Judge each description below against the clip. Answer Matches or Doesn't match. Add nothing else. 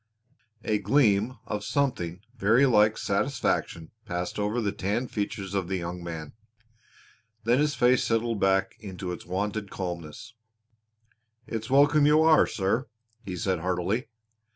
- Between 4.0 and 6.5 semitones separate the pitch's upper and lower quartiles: Matches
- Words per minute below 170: Matches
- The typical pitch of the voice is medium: Doesn't match